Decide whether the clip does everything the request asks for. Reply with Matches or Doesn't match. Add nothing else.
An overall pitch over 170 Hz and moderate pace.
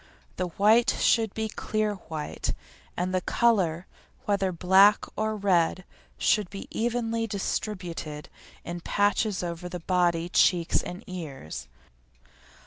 Doesn't match